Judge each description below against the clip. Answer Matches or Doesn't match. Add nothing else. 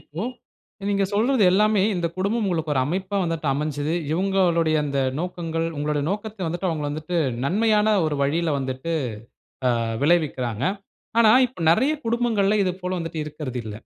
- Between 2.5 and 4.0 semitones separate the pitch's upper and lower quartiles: Doesn't match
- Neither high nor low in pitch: Matches